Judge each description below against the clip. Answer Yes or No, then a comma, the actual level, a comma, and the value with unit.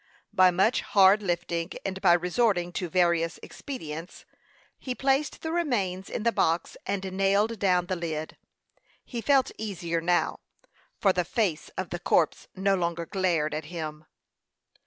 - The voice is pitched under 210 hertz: Yes, medium, 185 Hz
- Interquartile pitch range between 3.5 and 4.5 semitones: No, average, 3.1 semitones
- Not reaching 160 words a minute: Yes, average, 150 wpm